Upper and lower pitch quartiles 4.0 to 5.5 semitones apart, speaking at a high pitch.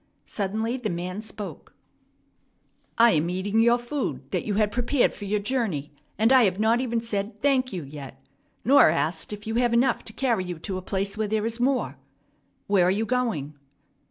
Yes: average, 4.3 semitones; high, 215 Hz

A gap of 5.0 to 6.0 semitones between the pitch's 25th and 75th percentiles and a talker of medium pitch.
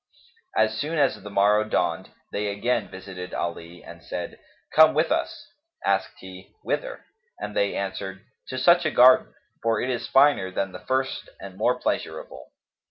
No: wide, 5.4 semitones; low, 110 Hz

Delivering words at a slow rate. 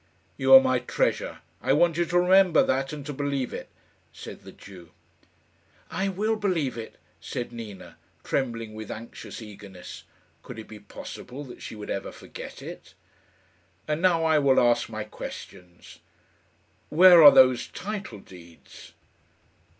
No: average, 150 wpm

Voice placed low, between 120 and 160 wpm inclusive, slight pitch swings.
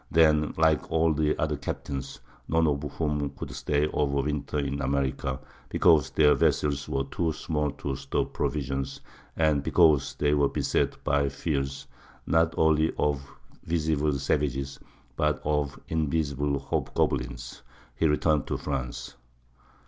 Yes: very low, 75 Hz; slow, 135 wpm; narrow, 2.1 semitones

